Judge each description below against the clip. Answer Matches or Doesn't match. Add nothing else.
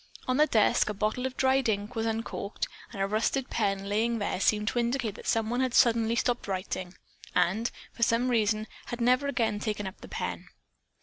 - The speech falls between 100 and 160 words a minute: Doesn't match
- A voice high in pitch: Matches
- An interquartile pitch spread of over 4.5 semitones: Doesn't match